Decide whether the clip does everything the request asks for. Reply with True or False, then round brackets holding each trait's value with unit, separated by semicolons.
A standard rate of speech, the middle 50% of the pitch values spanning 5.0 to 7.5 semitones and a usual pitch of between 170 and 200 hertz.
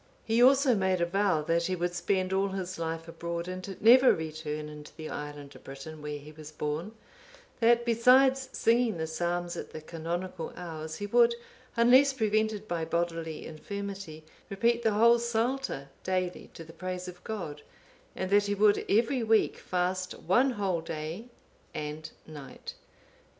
True (160 wpm; 5.3 semitones; 185 Hz)